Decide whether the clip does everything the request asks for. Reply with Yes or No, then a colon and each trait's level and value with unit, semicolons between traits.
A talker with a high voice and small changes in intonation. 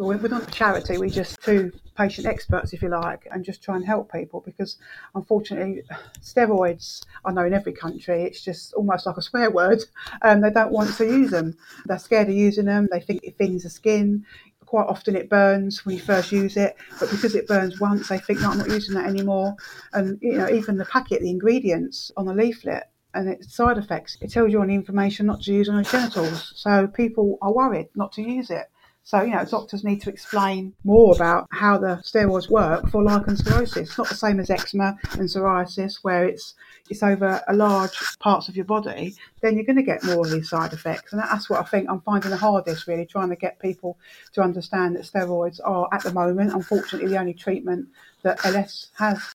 Yes: high, 195 Hz; narrow, 2.2 semitones